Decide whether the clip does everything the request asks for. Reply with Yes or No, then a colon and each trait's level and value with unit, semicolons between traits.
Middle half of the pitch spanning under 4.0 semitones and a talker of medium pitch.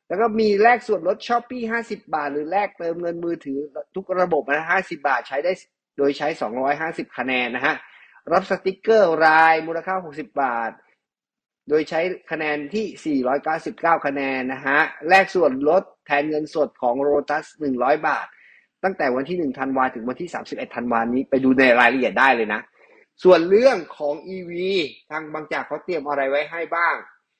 No: average, 4.9 semitones; medium, 160 Hz